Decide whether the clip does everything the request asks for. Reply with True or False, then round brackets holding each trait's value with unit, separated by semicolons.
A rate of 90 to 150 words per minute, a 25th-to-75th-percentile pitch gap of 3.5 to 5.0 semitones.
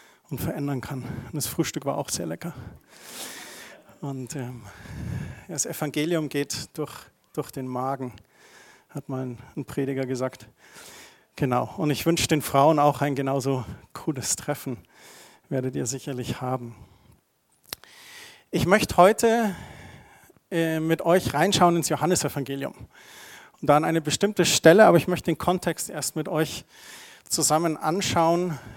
True (130 wpm; 3.9 semitones)